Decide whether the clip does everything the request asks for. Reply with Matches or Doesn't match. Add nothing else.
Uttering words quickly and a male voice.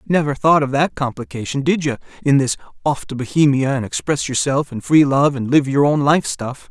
Matches